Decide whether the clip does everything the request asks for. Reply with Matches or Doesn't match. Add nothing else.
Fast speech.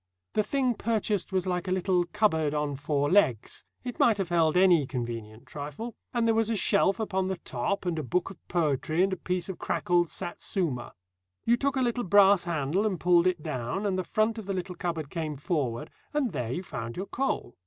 Matches